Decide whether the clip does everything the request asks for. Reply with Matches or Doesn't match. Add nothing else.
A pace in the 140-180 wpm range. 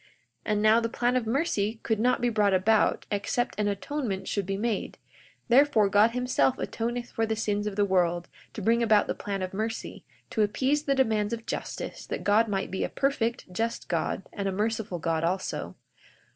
Doesn't match